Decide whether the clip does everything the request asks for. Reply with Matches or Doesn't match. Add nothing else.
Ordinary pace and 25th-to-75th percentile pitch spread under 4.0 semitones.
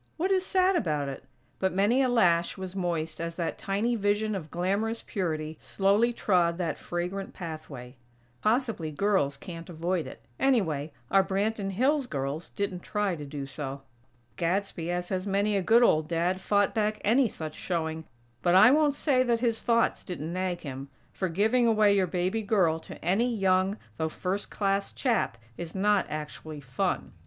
Doesn't match